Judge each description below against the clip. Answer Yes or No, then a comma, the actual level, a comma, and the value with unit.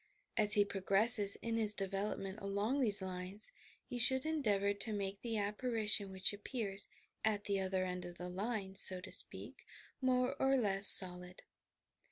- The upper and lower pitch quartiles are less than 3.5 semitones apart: Yes, average, 2.8 semitones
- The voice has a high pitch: Yes, high, 205 Hz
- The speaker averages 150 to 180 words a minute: Yes, average, 165 wpm